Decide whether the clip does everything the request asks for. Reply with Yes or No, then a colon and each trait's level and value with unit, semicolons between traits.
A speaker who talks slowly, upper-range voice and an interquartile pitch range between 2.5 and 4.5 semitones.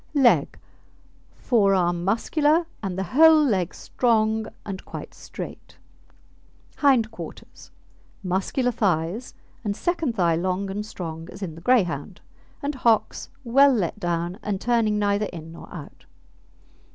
No: slow, 125 wpm; high, 210 Hz; average, 5.3 semitones